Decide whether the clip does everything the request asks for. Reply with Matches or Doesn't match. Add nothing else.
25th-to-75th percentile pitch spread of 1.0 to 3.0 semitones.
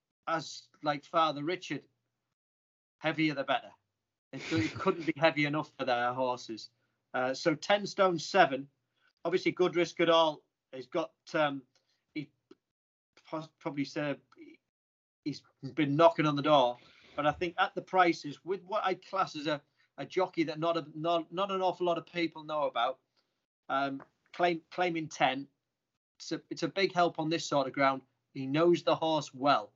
Doesn't match